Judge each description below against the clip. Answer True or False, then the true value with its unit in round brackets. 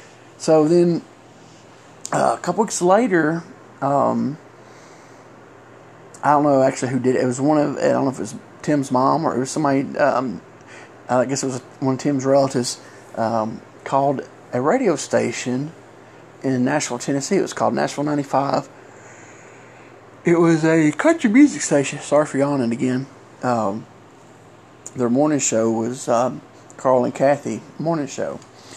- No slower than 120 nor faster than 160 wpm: True (155 wpm)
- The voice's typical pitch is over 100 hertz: True (135 Hz)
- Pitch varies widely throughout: False (3.1 semitones)